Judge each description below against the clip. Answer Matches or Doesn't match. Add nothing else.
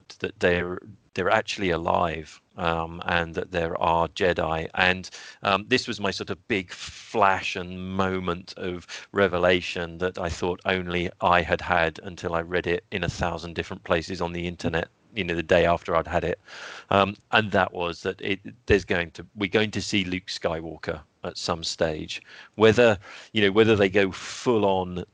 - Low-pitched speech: Matches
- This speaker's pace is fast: Doesn't match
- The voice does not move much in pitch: Matches